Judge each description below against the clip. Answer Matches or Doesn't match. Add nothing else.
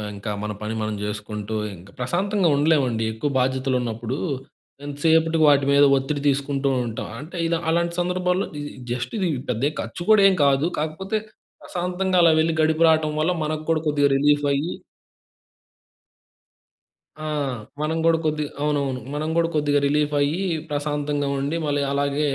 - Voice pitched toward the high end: Doesn't match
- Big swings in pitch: Doesn't match